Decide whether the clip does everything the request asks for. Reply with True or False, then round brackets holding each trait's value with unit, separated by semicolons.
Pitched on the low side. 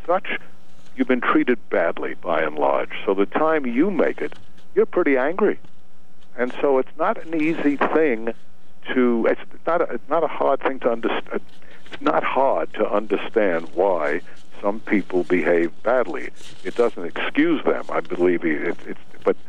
False (145 Hz)